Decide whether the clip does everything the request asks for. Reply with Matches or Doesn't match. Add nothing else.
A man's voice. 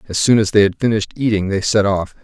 Matches